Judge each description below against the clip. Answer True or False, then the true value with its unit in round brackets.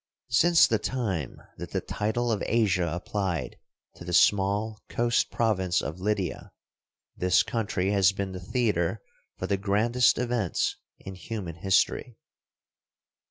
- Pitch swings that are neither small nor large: True (3.6 semitones)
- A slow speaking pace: True (130 wpm)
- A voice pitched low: True (100 Hz)